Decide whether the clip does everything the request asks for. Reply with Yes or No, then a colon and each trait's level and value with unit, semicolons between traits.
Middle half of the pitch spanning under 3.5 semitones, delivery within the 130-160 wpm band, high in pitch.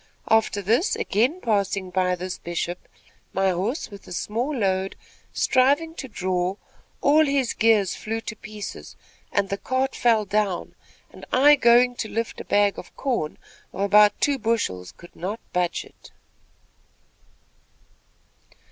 No: average, 4.7 semitones; average, 140 wpm; high, 210 Hz